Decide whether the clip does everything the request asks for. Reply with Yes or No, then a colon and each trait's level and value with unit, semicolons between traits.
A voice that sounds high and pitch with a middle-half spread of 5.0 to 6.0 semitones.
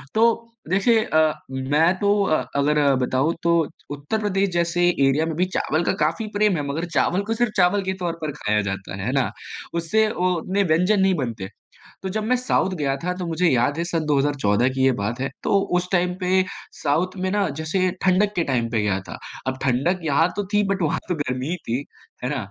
No: medium, 165 Hz; wide, 5.6 semitones